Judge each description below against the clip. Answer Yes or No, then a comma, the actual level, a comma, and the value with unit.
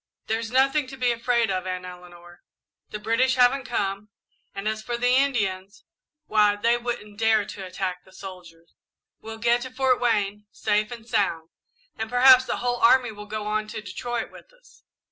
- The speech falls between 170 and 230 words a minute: Yes, average, 180 wpm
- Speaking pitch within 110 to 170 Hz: No, high, 220 Hz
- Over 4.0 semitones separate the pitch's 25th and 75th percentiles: No, average, 3.7 semitones